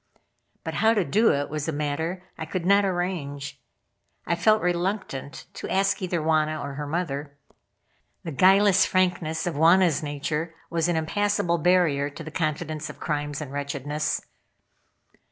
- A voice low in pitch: No, medium, 160 Hz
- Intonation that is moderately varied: Yes, average, 3.8 semitones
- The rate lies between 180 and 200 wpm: No, average, 155 wpm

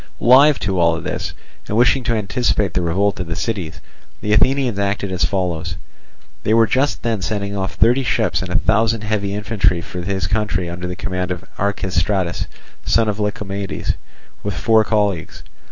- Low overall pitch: Yes, low, 100 Hz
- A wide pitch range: No, average, 3.3 semitones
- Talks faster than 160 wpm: Yes, average, 170 wpm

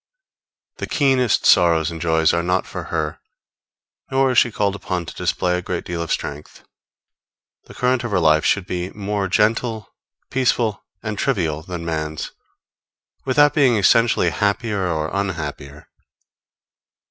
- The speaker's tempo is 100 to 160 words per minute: Yes, average, 145 wpm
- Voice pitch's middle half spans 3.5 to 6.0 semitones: Yes, wide, 5.5 semitones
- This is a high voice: No, very low, 95 Hz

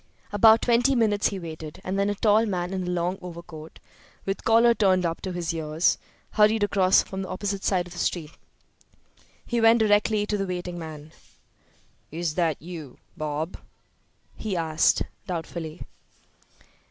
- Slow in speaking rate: No, average, 155 wpm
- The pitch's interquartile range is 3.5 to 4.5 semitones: Yes, average, 3.8 semitones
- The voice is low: No, medium, 185 Hz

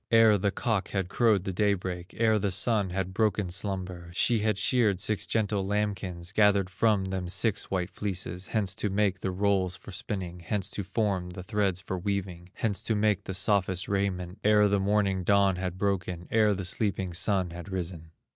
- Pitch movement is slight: Yes, narrow, 2.2 semitones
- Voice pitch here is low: Yes, very low, 95 Hz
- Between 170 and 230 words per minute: Yes, average, 190 wpm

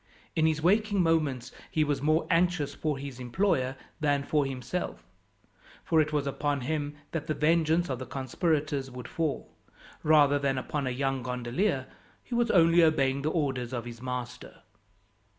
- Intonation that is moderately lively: Yes, average, 3.4 semitones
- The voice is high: No, medium, 145 Hz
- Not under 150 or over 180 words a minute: Yes, average, 165 wpm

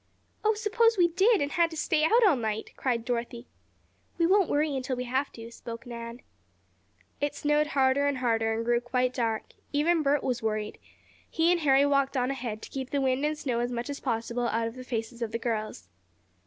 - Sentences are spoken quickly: Yes, fast, 210 wpm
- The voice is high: Yes, very high, 260 Hz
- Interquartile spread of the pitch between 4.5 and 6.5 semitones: No, average, 4.1 semitones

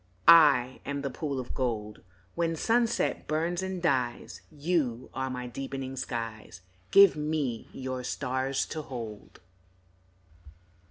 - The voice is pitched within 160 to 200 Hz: No, low, 135 Hz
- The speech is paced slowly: Yes, slow, 120 wpm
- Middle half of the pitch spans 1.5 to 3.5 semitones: No, average, 4.1 semitones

